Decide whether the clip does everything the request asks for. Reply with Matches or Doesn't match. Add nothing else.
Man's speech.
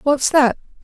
Doesn't match